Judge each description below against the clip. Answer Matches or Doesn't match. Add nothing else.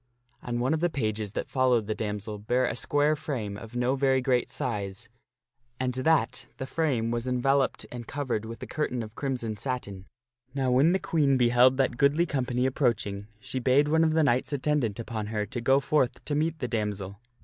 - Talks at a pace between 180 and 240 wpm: Matches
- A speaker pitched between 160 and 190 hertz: Doesn't match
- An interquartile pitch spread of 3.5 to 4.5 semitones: Matches